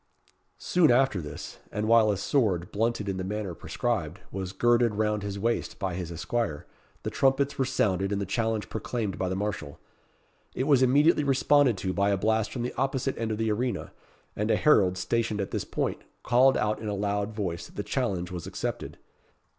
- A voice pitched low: Yes, low, 105 Hz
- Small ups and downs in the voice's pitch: No, average, 3.8 semitones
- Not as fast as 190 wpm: No, average, 195 wpm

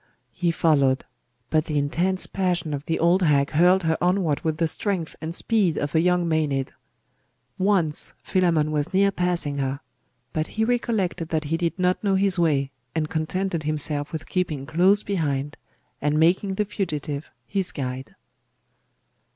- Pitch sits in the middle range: Yes, medium, 165 Hz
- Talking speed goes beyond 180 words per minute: No, average, 160 wpm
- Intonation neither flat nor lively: Yes, average, 3.7 semitones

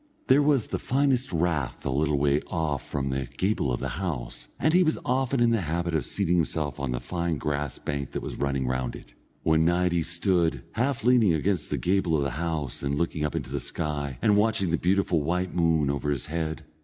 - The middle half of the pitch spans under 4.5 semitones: No, average, 5.0 semitones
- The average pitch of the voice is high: No, very low, 80 Hz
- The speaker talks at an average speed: No, fast, 220 wpm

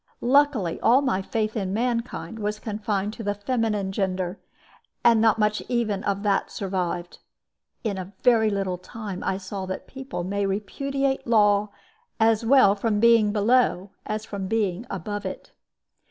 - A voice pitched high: Yes, high, 210 Hz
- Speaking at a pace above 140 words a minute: Yes, average, 155 wpm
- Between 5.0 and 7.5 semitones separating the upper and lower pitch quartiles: No, average, 2.7 semitones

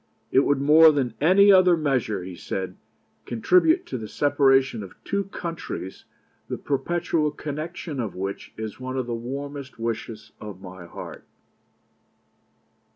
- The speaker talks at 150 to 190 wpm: No, average, 140 wpm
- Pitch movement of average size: No, wide, 6.3 semitones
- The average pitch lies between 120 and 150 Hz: Yes, low, 135 Hz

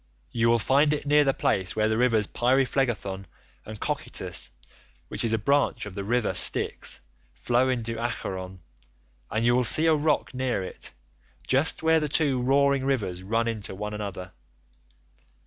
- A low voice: Yes, low, 120 Hz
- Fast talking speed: No, average, 165 wpm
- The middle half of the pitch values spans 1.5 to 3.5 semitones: No, average, 4.5 semitones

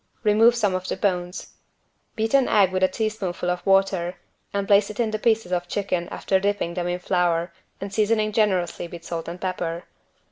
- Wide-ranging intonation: No, average, 3.1 semitones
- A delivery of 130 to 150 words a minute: No, average, 190 wpm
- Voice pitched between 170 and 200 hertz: Yes, high, 190 Hz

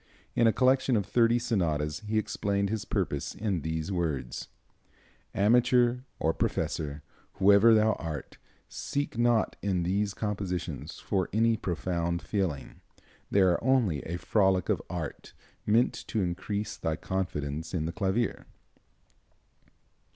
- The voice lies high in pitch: No, low, 100 Hz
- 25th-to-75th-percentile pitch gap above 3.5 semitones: Yes, average, 4.6 semitones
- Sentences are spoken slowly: Yes, slow, 130 wpm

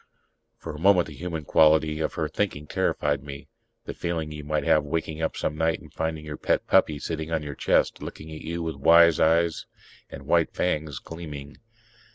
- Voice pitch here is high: No, very low, 80 Hz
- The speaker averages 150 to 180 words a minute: No, average, 195 wpm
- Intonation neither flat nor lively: No, narrow, 1.6 semitones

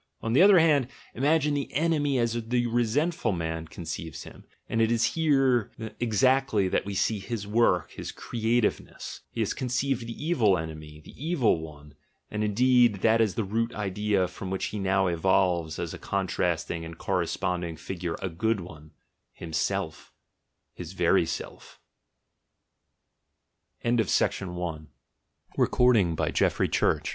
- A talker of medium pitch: No, low, 105 Hz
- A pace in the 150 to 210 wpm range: No, slow, 135 wpm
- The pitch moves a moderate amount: No, wide, 5.8 semitones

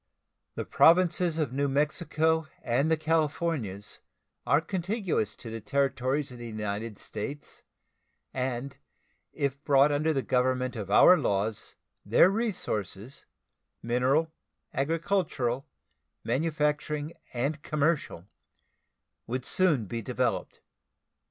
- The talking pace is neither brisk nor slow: No, slow, 105 wpm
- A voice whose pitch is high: No, medium, 140 Hz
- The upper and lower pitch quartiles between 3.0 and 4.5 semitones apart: No, average, 4.9 semitones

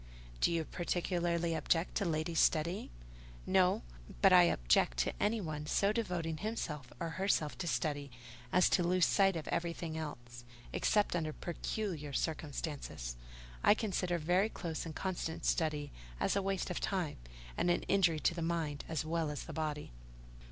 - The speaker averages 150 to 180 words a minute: Yes, average, 160 wpm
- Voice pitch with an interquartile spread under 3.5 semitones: Yes, average, 2.8 semitones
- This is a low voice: No, medium, 170 Hz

